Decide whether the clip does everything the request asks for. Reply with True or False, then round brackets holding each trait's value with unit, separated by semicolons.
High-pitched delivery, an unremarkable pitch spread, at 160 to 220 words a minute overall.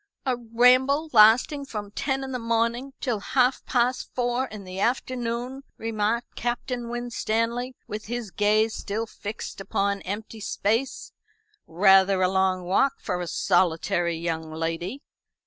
False (225 Hz; 4.1 semitones; 135 wpm)